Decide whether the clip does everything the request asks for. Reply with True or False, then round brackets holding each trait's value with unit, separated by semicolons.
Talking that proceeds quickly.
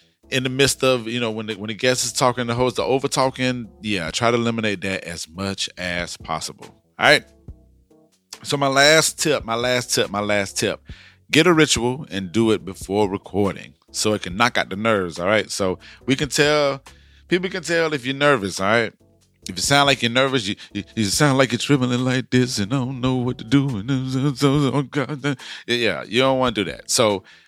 True (215 wpm)